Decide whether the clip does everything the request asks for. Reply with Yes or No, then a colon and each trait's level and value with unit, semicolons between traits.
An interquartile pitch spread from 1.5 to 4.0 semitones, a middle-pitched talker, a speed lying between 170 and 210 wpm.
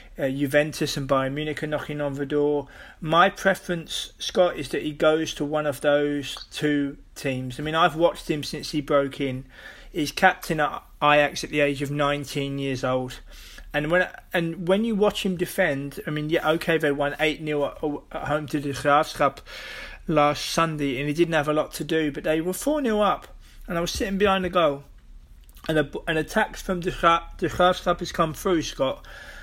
Yes: average, 3.0 semitones; medium, 150 Hz; average, 200 wpm